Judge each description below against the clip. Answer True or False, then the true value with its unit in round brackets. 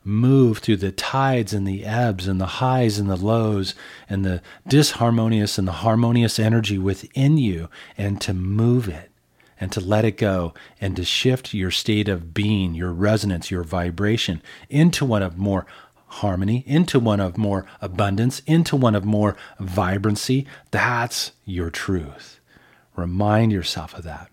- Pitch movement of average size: True (3.4 semitones)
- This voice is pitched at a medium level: False (105 Hz)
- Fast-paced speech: False (160 wpm)